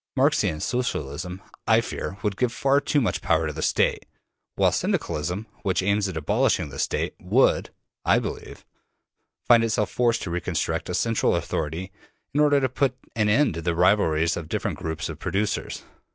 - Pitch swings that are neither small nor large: No, wide, 6.2 semitones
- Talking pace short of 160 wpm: No, average, 170 wpm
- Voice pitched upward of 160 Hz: No, low, 100 Hz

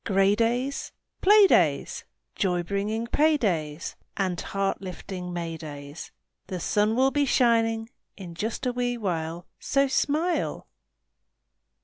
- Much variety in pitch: Yes, wide, 5.8 semitones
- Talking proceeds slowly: Yes, slow, 125 wpm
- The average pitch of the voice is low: No, high, 205 Hz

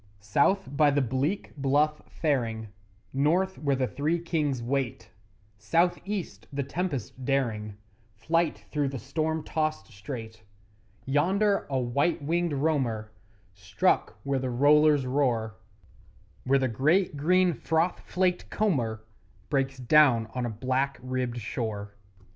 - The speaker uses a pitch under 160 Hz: Yes, medium, 140 Hz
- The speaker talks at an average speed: No, slow, 125 wpm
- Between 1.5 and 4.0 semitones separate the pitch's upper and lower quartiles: No, average, 4.6 semitones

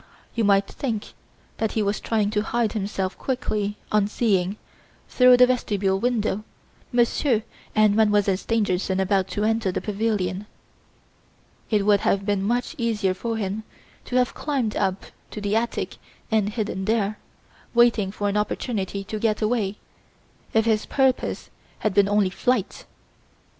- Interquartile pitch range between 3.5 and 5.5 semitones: No, narrow, 2.4 semitones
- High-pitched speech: Yes, high, 210 Hz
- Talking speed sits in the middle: Yes, average, 150 wpm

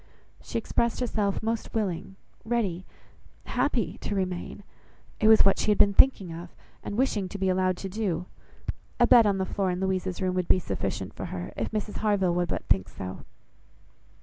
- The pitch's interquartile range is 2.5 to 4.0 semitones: Yes, average, 2.8 semitones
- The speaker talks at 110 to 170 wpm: No, average, 185 wpm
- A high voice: Yes, high, 195 Hz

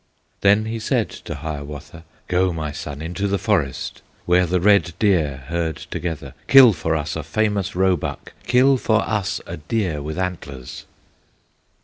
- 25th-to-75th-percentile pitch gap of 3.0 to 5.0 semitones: Yes, average, 4.7 semitones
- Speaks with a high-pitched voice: No, very low, 90 Hz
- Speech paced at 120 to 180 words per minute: Yes, average, 150 wpm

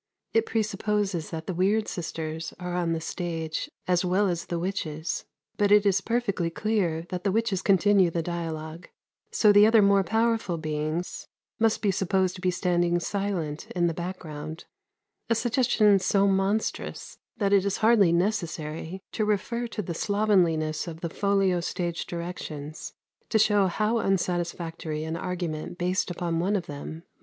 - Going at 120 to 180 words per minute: Yes, average, 165 wpm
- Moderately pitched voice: Yes, medium, 180 Hz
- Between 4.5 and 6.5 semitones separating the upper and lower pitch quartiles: No, average, 3.5 semitones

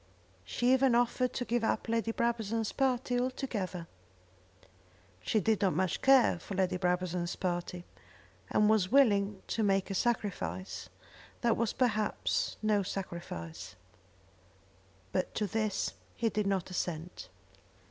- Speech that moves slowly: Yes, slow, 125 wpm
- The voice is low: No, high, 210 Hz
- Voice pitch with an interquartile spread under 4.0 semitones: No, average, 4.5 semitones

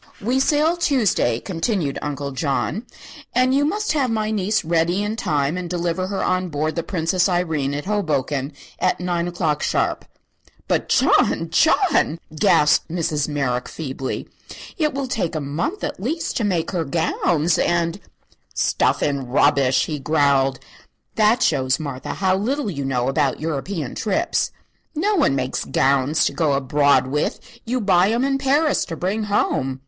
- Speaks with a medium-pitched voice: Yes, medium, 170 Hz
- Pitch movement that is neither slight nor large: No, wide, 6.9 semitones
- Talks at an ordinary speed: Yes, average, 160 wpm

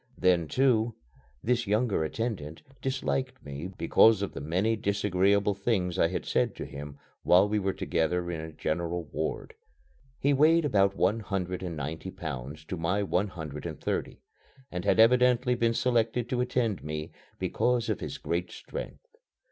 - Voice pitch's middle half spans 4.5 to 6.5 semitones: Yes, wide, 5.6 semitones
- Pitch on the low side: Yes, low, 100 Hz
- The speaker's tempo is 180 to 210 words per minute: No, average, 165 wpm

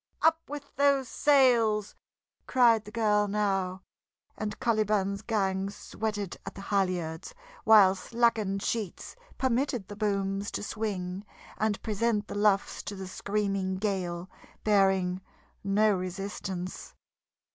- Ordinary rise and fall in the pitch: No, narrow, 2.3 semitones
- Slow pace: Yes, slow, 115 wpm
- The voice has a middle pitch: No, high, 205 Hz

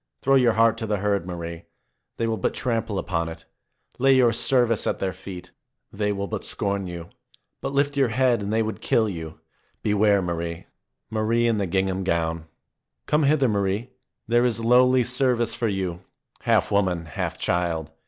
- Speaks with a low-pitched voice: Yes, low, 105 Hz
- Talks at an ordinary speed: Yes, average, 180 wpm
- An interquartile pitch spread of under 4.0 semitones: No, average, 4.8 semitones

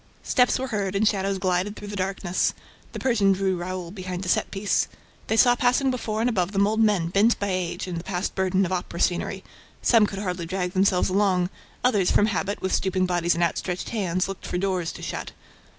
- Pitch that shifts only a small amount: Yes, narrow, 2.3 semitones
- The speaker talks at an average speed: No, fast, 215 wpm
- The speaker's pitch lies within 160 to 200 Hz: Yes, high, 190 Hz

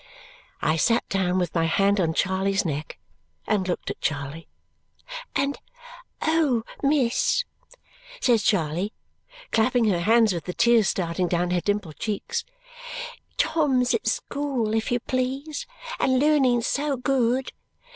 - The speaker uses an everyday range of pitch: No, wide, 6.3 semitones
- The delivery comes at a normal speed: No, slow, 130 wpm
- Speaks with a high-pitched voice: Yes, high, 220 Hz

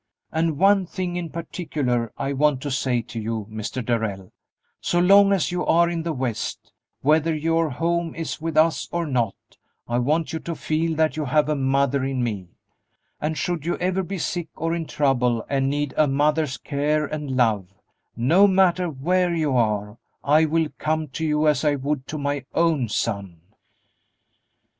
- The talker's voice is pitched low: No, medium, 150 Hz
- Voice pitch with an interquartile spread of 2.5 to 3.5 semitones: No, average, 4.2 semitones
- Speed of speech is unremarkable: Yes, average, 180 wpm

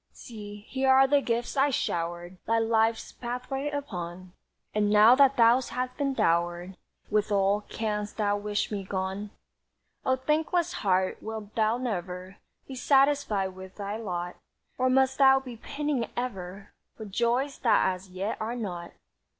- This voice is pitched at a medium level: No, high, 220 Hz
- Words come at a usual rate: Yes, average, 150 wpm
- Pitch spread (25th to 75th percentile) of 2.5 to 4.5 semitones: No, average, 5.1 semitones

